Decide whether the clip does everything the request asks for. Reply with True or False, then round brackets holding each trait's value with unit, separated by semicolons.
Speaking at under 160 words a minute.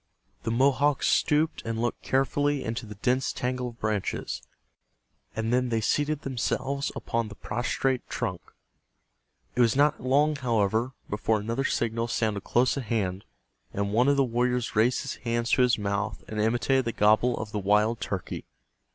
False (165 wpm)